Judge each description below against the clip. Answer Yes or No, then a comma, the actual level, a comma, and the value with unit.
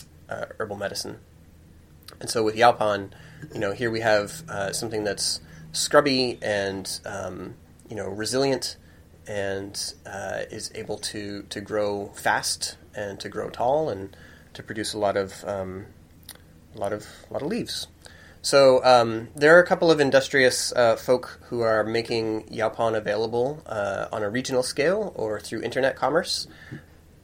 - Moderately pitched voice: No, low, 100 Hz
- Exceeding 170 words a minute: No, average, 155 wpm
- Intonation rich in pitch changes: Yes, wide, 5.7 semitones